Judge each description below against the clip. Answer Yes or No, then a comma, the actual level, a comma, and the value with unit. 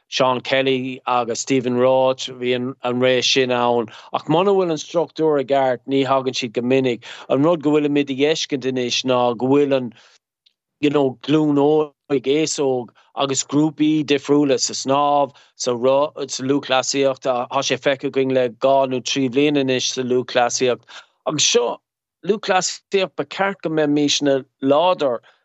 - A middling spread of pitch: No, narrow, 2.3 semitones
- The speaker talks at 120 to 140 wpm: Yes, slow, 135 wpm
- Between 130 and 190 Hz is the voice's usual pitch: Yes, low, 135 Hz